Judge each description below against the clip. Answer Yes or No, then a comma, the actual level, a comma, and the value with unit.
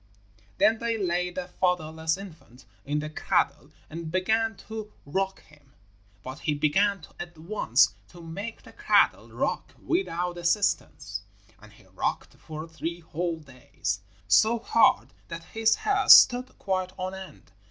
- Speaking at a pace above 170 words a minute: No, average, 140 wpm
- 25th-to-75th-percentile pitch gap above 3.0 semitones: Yes, average, 4.8 semitones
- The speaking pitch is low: No, medium, 175 Hz